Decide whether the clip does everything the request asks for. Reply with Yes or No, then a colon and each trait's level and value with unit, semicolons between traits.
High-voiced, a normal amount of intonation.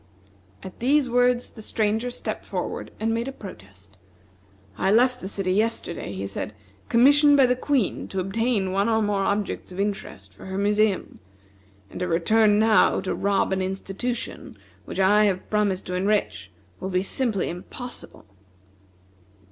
Yes: high, 205 Hz; average, 3.7 semitones